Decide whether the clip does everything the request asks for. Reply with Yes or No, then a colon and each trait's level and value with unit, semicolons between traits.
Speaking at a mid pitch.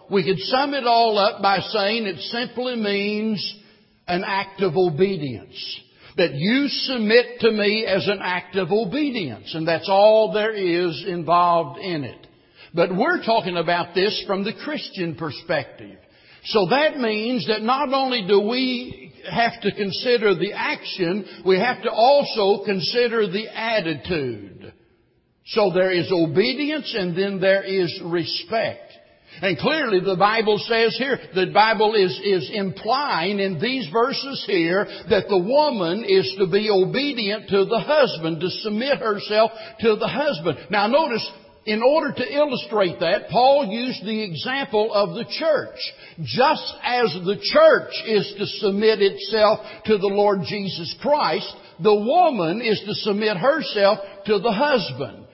No: high, 205 Hz